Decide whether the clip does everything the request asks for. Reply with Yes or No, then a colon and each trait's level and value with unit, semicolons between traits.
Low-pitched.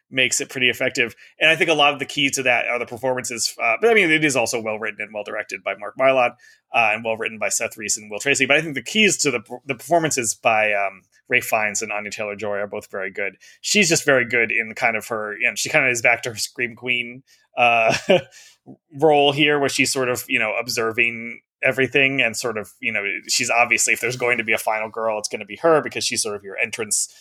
Yes: low, 120 Hz